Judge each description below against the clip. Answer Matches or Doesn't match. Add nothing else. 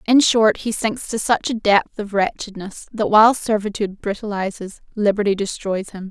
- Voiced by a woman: Matches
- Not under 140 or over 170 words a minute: Matches